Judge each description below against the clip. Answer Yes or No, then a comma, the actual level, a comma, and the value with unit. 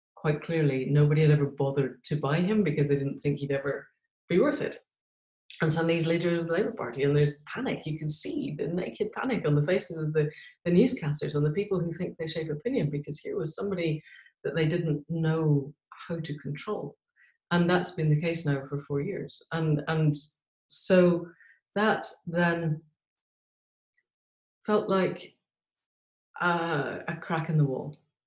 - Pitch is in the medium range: Yes, medium, 155 Hz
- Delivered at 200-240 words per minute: No, average, 175 wpm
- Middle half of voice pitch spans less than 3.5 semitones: Yes, average, 2.8 semitones